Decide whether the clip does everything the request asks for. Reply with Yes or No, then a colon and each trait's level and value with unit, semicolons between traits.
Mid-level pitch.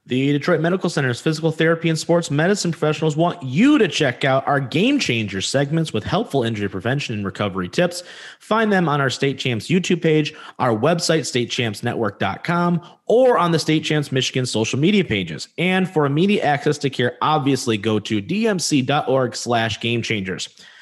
Yes: medium, 145 Hz